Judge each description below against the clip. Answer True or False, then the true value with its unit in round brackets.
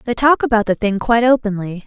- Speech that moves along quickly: True (225 wpm)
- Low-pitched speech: False (220 Hz)